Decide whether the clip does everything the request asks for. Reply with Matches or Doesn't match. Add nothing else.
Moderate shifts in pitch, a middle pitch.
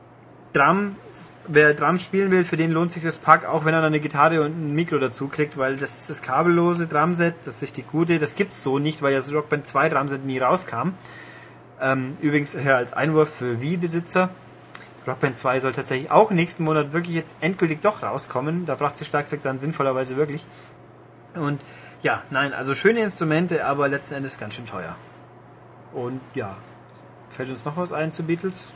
Matches